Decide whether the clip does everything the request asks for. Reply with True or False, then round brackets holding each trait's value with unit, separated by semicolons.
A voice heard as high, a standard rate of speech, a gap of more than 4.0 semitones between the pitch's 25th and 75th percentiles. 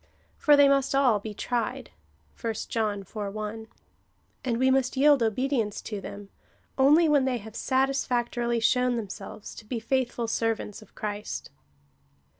False (235 Hz; 150 wpm; 3.6 semitones)